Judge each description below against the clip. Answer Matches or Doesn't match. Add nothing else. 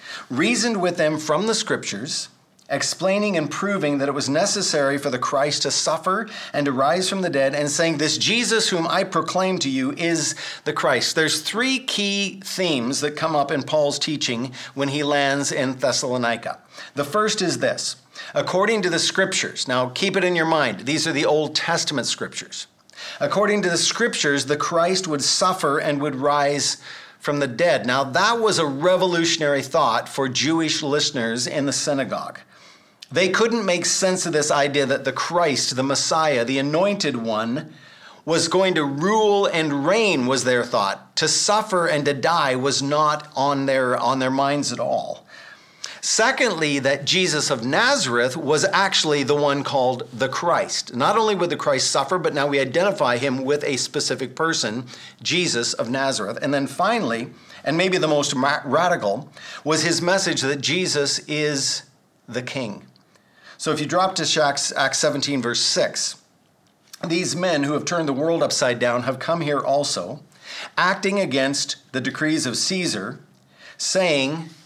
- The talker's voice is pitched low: Doesn't match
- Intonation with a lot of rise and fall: Doesn't match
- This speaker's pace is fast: Doesn't match